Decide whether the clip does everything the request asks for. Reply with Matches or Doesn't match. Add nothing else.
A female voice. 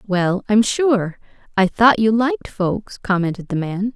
Matches